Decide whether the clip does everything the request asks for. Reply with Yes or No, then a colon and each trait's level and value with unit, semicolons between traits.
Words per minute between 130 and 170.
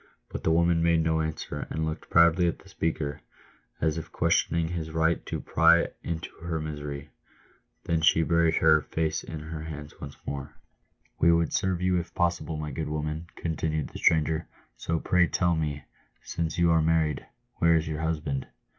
No: average, 180 wpm